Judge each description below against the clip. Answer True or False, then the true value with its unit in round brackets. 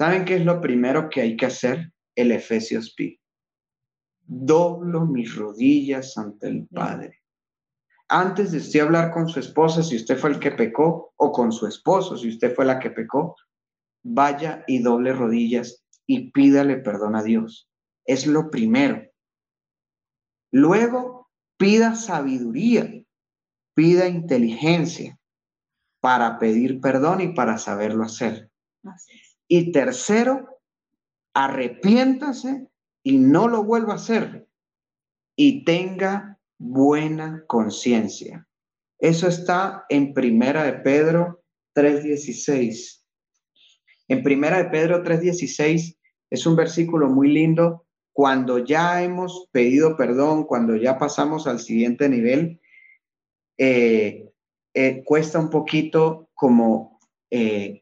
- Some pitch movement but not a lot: False (5.9 semitones)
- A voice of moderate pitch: True (155 Hz)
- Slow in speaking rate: True (115 wpm)